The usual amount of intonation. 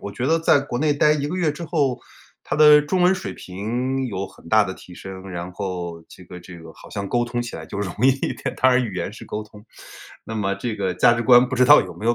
No: wide, 6.1 semitones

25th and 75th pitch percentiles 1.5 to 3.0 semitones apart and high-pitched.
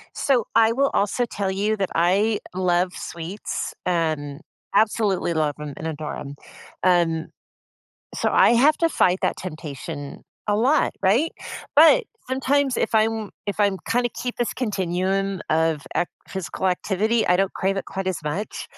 No: average, 4.6 semitones; high, 195 Hz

